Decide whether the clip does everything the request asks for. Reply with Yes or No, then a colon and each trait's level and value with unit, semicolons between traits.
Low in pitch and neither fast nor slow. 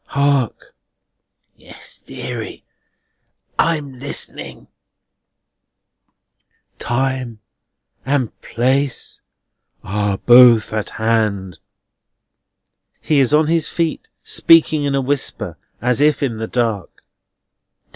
No: low, 130 Hz; slow, 90 wpm